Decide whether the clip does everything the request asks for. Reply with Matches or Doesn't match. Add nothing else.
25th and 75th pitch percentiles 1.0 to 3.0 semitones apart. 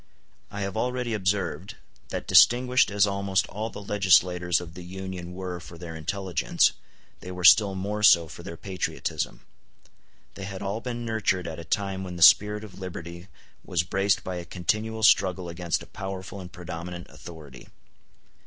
Matches